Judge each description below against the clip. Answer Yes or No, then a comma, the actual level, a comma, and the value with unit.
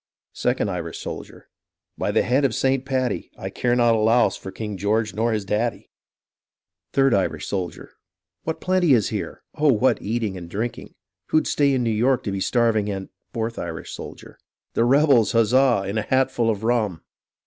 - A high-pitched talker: No, low, 115 Hz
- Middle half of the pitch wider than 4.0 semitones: No, average, 3.7 semitones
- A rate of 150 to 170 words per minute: No, average, 185 wpm